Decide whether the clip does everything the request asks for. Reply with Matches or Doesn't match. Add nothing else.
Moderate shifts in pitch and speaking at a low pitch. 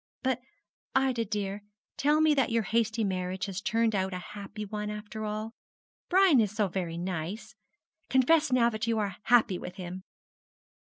Doesn't match